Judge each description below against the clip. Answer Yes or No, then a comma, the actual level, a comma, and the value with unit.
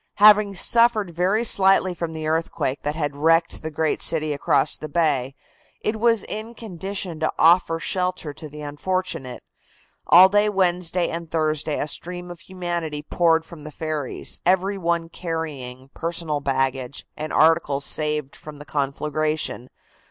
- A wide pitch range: No, average, 3.4 semitones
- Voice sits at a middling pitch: Yes, medium, 165 Hz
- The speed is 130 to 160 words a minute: Yes, average, 150 wpm